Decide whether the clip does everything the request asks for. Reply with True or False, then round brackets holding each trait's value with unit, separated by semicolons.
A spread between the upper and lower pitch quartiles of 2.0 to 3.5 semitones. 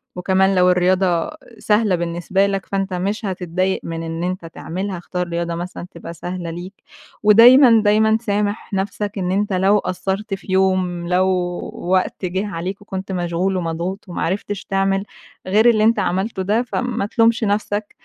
True (2.4 semitones)